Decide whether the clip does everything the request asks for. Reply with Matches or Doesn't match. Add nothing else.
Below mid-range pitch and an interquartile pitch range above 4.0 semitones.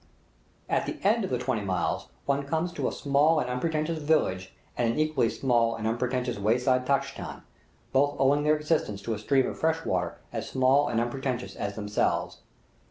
Matches